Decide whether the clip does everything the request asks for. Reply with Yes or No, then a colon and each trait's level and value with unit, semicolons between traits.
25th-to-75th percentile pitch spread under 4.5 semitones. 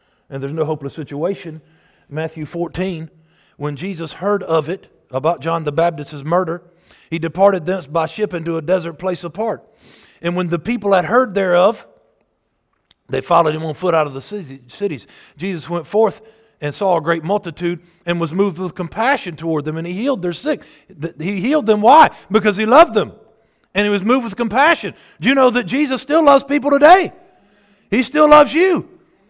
No: average, 4.9 semitones